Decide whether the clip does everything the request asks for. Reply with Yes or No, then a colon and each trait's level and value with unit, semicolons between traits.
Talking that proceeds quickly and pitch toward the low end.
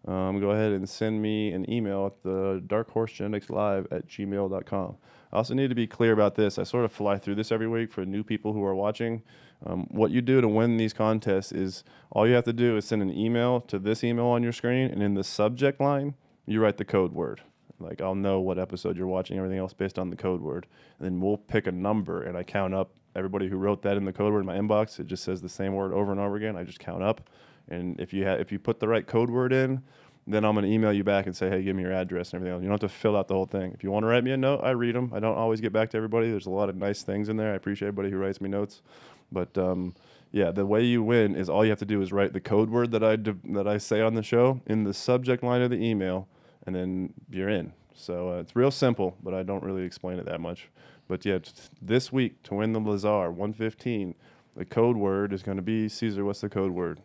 Yes: fast, 275 wpm; low, 105 Hz